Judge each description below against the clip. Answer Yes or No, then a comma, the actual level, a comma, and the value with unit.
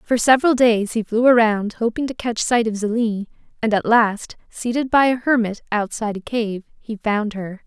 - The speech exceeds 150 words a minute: Yes, average, 195 wpm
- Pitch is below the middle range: No, high, 225 Hz